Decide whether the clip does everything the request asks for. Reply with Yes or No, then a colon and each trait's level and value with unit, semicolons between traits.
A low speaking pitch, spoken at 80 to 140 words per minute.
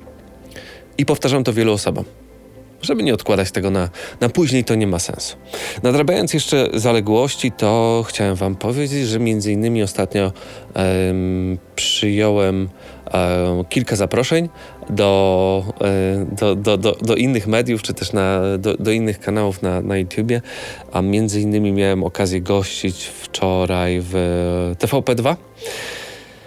Yes: low, 100 Hz; average, 135 wpm